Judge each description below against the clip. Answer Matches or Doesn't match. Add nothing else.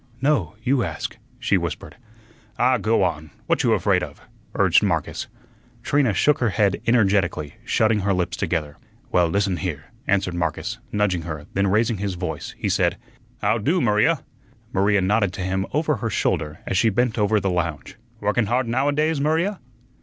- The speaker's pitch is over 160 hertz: Doesn't match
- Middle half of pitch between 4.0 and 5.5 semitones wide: Matches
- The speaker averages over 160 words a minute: Matches